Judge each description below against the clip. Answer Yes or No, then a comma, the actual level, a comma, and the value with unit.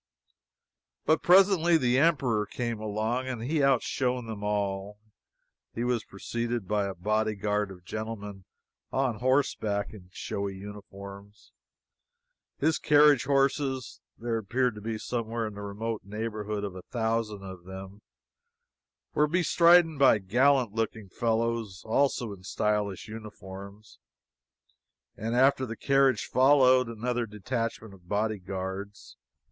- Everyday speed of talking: No, slow, 120 wpm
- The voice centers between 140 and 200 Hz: No, low, 110 Hz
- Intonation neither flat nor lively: Yes, average, 3.8 semitones